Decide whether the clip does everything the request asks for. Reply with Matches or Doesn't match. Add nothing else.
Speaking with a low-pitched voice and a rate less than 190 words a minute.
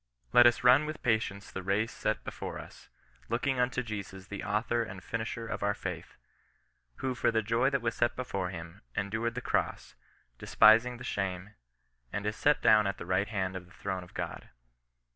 Doesn't match